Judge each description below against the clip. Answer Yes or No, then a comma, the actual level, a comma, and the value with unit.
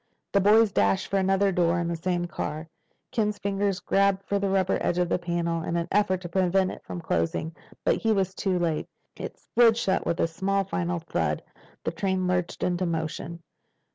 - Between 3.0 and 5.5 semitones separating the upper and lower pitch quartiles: No, narrow, 2.6 semitones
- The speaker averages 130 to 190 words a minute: No, average, 200 wpm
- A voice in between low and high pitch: Yes, medium, 180 Hz